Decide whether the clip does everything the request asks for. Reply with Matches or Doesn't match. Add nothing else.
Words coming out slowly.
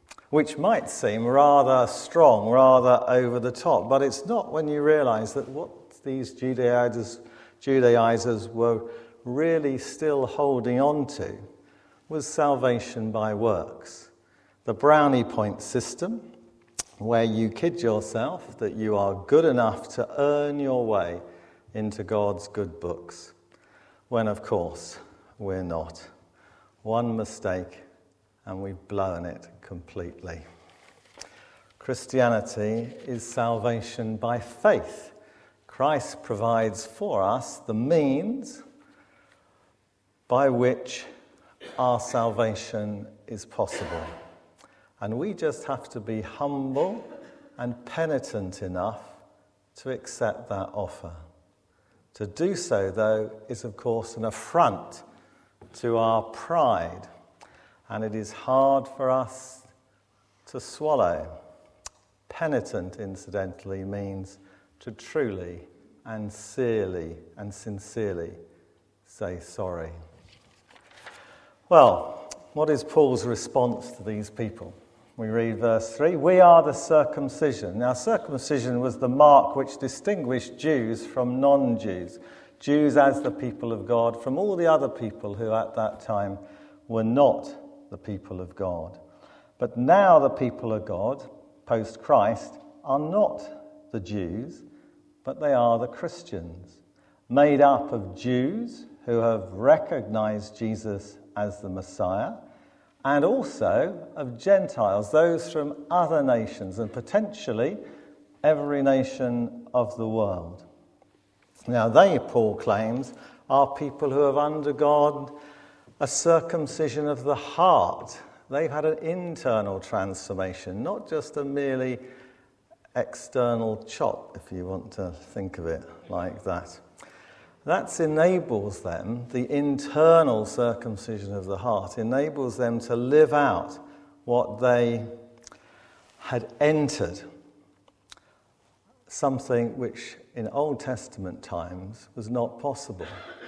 Matches